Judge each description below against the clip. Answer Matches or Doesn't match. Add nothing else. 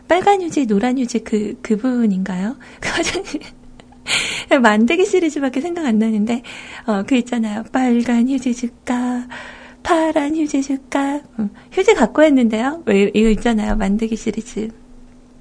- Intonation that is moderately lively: Matches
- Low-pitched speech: Doesn't match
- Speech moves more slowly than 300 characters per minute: Matches